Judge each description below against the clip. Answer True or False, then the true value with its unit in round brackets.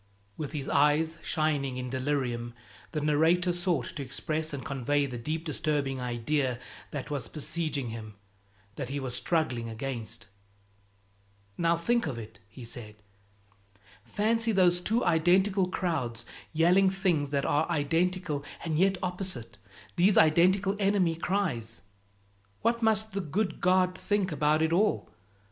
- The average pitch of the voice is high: False (155 Hz)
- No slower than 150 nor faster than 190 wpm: False (135 wpm)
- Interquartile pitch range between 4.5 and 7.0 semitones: True (5.4 semitones)